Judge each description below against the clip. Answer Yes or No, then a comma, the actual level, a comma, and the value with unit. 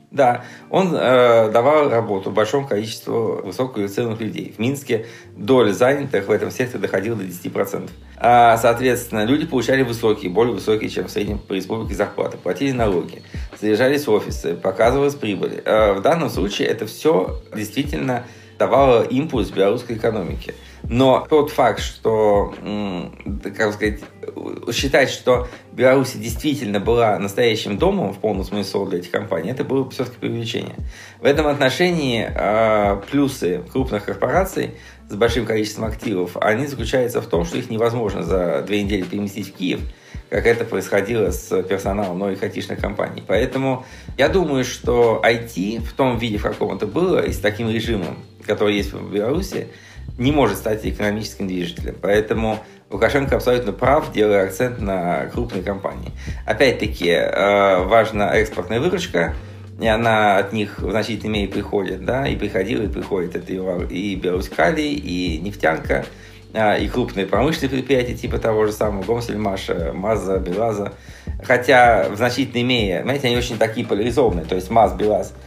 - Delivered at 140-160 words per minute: Yes, average, 145 wpm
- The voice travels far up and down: No, average, 3.7 semitones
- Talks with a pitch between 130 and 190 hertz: No, low, 110 Hz